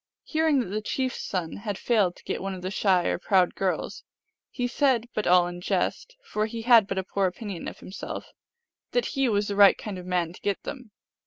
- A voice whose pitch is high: Yes, high, 205 Hz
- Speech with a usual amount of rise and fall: Yes, average, 4.4 semitones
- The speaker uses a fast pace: Yes, fast, 235 wpm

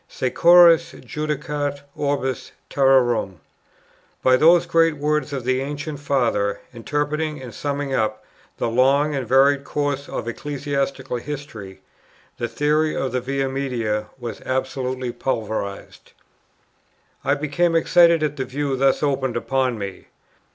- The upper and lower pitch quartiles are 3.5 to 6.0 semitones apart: No, narrow, 2.6 semitones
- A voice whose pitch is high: No, low, 135 Hz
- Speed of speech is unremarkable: No, slow, 125 wpm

